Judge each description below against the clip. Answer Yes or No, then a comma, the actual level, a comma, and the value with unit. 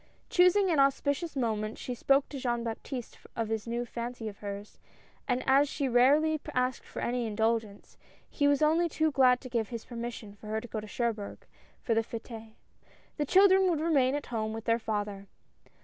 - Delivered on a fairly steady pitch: No, average, 4.2 semitones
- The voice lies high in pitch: Yes, high, 240 Hz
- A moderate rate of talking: Yes, average, 190 wpm